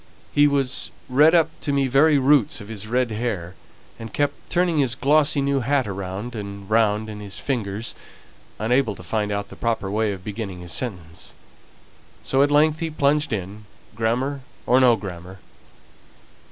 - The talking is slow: No, average, 165 wpm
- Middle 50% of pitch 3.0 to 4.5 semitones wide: No, wide, 5.5 semitones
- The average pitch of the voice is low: Yes, low, 115 Hz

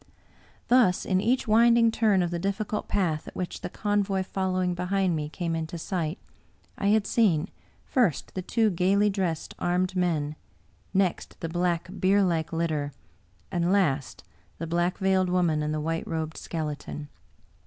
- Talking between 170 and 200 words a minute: No, average, 155 wpm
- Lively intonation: No, average, 3.2 semitones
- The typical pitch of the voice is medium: Yes, medium, 180 Hz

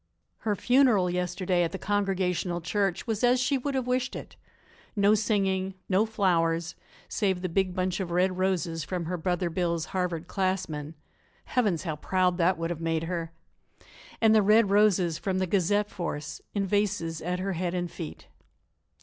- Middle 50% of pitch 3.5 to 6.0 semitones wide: No, average, 3.0 semitones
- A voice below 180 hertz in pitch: No, medium, 185 Hz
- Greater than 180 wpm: No, average, 170 wpm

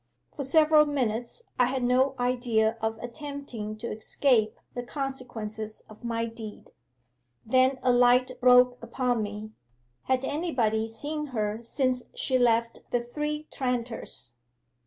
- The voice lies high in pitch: Yes, high, 245 Hz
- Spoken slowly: Yes, slow, 130 wpm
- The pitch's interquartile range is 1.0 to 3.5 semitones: Yes, average, 2.9 semitones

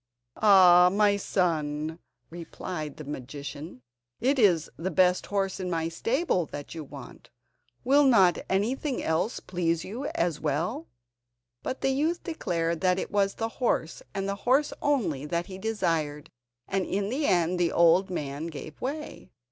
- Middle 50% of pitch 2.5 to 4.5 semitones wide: No, average, 5.0 semitones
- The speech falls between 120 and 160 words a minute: Yes, average, 155 wpm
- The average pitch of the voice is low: No, medium, 180 Hz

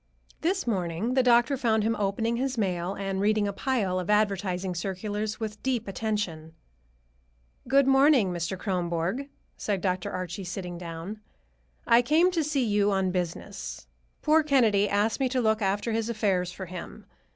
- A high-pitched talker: Yes, high, 205 Hz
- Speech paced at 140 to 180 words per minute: Yes, average, 160 wpm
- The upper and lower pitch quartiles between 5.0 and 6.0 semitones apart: No, average, 4.5 semitones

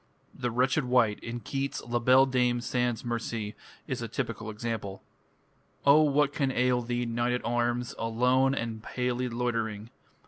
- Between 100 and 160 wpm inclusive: Yes, average, 150 wpm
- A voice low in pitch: Yes, low, 120 Hz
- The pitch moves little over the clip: Yes, narrow, 1.6 semitones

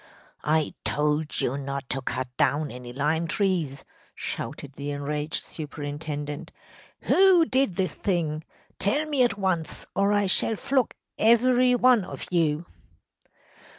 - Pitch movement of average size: No, wide, 6.7 semitones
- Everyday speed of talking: No, slow, 130 wpm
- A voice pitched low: No, medium, 160 Hz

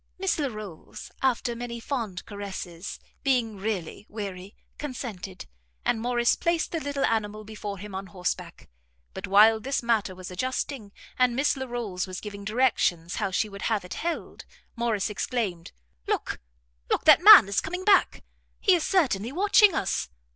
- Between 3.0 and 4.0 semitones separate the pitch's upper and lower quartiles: No, average, 5.0 semitones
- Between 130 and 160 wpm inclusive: Yes, average, 155 wpm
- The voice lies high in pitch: Yes, high, 220 Hz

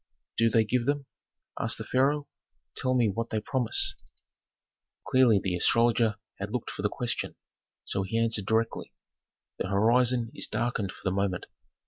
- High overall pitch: No, low, 115 Hz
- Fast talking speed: No, average, 155 wpm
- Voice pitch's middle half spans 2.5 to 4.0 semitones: Yes, average, 3.2 semitones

